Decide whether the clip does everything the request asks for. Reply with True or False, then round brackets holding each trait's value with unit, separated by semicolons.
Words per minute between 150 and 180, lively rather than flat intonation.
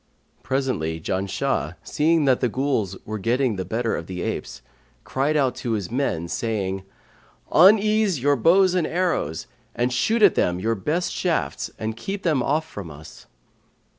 True (160 wpm; 8.2 semitones)